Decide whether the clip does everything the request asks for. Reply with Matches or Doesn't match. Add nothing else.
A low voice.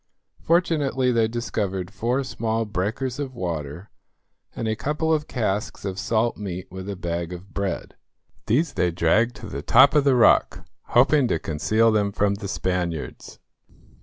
Matches